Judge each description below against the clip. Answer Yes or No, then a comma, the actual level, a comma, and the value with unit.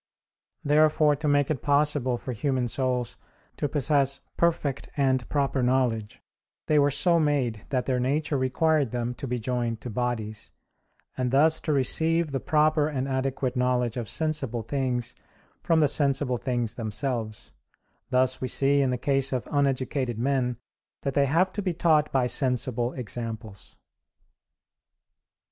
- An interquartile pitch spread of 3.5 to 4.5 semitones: No, average, 3.0 semitones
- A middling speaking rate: Yes, average, 150 wpm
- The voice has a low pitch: Yes, low, 130 Hz